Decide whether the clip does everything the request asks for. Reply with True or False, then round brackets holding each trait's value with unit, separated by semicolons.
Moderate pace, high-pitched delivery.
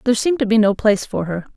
False (310 wpm; 220 Hz)